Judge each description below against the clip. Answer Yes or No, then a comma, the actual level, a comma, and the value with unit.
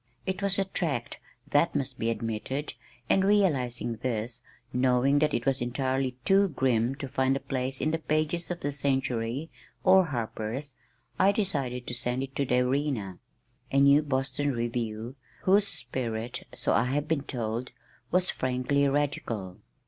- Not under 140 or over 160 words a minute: Yes, average, 155 wpm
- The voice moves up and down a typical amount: Yes, average, 3.4 semitones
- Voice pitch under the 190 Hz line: Yes, low, 135 Hz